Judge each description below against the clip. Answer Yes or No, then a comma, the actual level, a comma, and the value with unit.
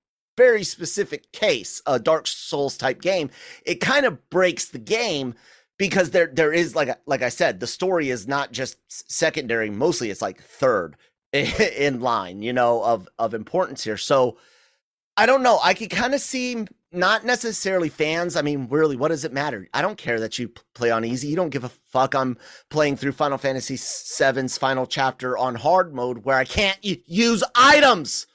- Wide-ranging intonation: Yes, wide, 6.4 semitones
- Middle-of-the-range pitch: Yes, medium, 145 Hz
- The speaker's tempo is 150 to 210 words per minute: Yes, average, 190 wpm